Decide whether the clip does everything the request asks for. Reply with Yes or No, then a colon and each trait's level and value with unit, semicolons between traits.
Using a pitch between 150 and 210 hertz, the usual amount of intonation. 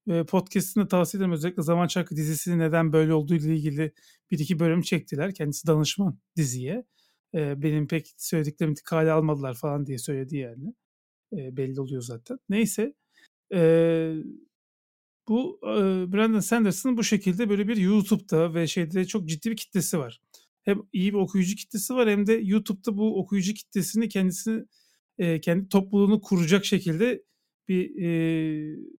Yes: medium, 185 Hz; average, 4.9 semitones